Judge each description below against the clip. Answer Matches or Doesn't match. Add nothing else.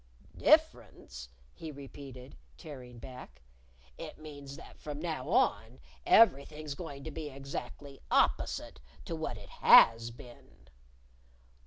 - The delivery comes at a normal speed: Doesn't match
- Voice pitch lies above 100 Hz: Matches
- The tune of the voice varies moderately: Matches